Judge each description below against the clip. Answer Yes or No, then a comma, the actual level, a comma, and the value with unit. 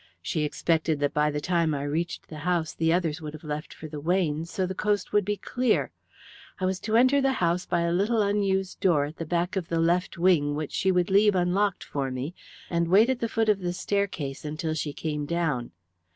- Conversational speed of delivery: No, fast, 225 wpm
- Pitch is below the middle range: No, medium, 170 Hz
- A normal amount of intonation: Yes, average, 3.8 semitones